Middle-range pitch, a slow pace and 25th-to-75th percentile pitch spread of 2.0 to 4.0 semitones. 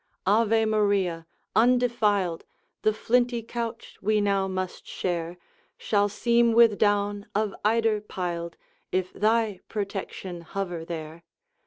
No: high, 205 Hz; slow, 115 wpm; average, 3.3 semitones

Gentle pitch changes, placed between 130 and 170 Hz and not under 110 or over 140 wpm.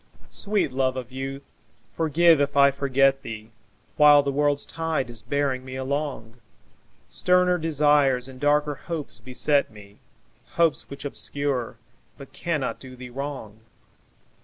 Yes: narrow, 2.3 semitones; medium, 140 Hz; slow, 135 wpm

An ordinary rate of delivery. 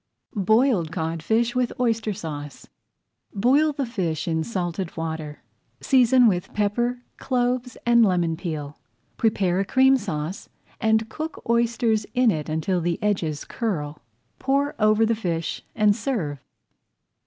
No: slow, 130 wpm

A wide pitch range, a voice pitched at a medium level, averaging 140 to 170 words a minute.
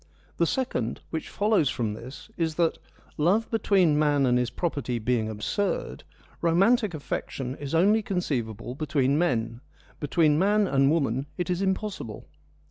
Yes: wide, 7.0 semitones; medium, 155 Hz; average, 145 wpm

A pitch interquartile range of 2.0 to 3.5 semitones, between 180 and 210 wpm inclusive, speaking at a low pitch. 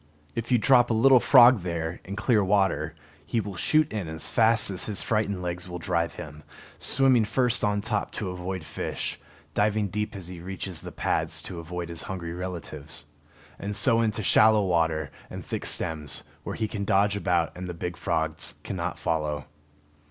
No: average, 4.2 semitones; average, 185 wpm; very low, 95 Hz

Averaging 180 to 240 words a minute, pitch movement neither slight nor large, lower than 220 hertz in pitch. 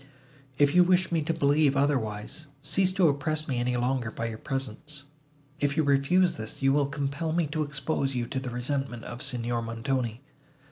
Yes: average, 185 wpm; average, 3.8 semitones; medium, 140 Hz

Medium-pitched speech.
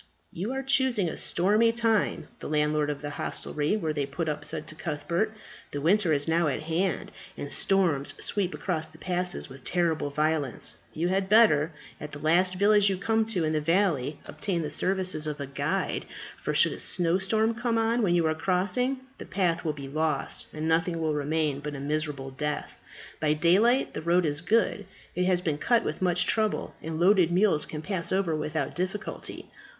Yes: medium, 170 Hz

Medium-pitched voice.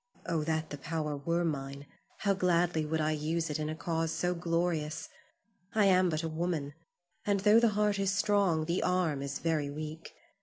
Yes: medium, 165 Hz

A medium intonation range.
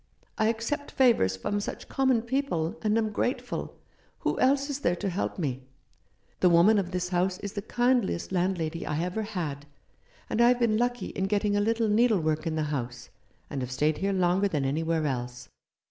No: wide, 6.1 semitones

